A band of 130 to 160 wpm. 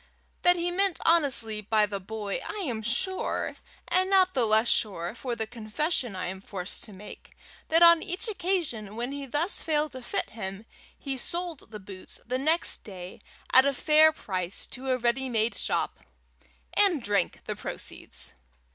No: average, 175 wpm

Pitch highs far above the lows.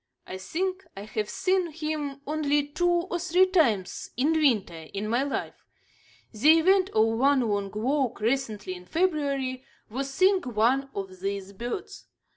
Yes: wide, 7.1 semitones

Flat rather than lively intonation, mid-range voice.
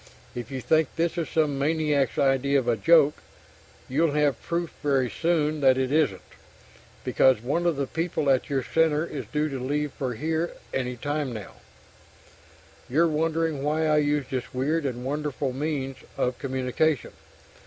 No: average, 3.1 semitones; medium, 145 Hz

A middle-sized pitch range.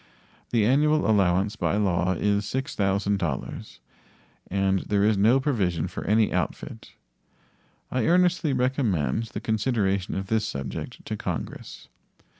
Yes: average, 4.2 semitones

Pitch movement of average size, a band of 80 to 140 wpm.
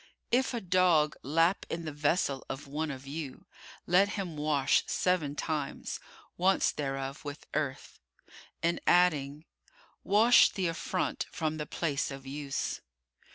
Yes: average, 4.0 semitones; slow, 135 wpm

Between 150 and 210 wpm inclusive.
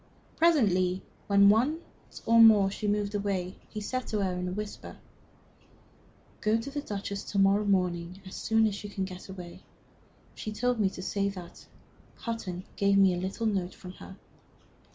Yes: average, 170 wpm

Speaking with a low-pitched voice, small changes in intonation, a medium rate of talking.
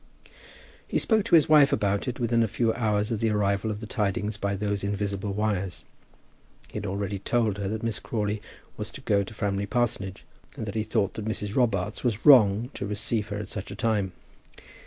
No: low, 105 Hz; narrow, 2.0 semitones; fast, 210 wpm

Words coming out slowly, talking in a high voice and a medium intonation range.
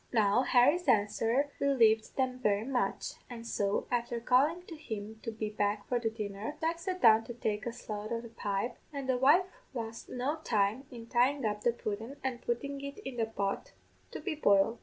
No: average, 200 wpm; high, 235 Hz; average, 3.8 semitones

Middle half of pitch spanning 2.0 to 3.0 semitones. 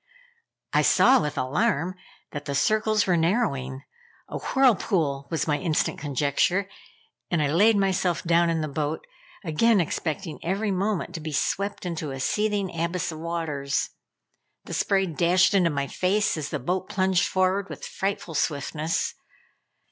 No: average, 4.3 semitones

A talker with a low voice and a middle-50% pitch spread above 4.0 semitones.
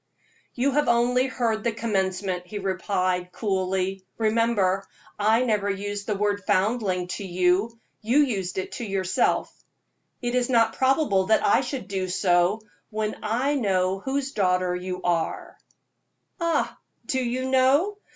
No: high, 205 Hz; average, 4.5 semitones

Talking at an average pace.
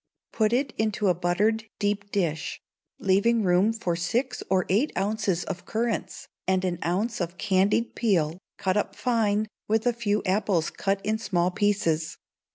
Yes: average, 160 wpm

